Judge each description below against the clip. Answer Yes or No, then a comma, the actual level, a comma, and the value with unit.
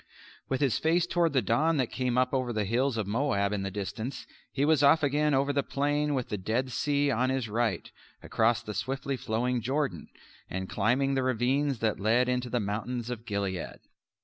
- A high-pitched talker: No, low, 125 Hz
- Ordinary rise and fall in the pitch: Yes, average, 4.1 semitones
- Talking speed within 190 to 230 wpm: Yes, average, 200 wpm